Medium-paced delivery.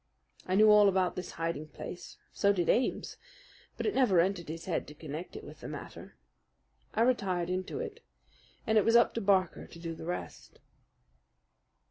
Yes: average, 180 wpm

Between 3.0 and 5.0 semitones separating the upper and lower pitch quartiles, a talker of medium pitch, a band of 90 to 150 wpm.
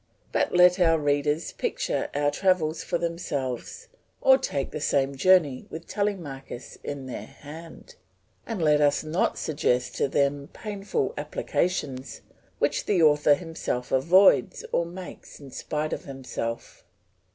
Yes: average, 4.2 semitones; medium, 155 Hz; slow, 135 wpm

